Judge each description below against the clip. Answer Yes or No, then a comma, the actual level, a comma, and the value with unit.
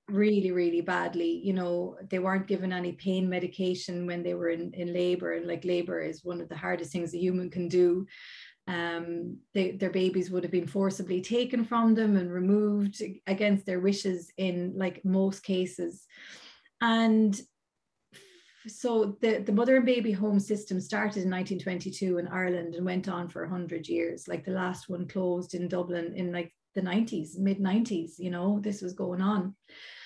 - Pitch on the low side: No, medium, 185 Hz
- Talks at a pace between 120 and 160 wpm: No, average, 180 wpm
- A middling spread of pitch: No, narrow, 2.0 semitones